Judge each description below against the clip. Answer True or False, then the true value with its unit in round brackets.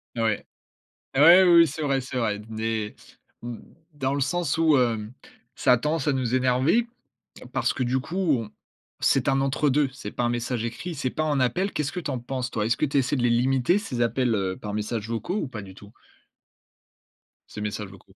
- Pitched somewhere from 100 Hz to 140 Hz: True (130 Hz)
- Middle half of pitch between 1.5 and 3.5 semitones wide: False (4.2 semitones)